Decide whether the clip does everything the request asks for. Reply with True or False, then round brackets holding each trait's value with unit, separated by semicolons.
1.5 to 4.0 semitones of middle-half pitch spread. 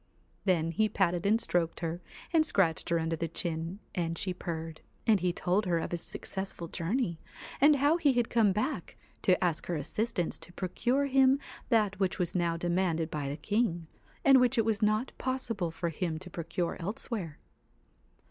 False (5.1 semitones)